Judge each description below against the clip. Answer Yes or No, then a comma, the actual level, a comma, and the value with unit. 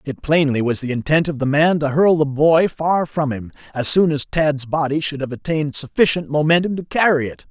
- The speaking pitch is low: No, medium, 150 Hz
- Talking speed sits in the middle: No, fast, 225 wpm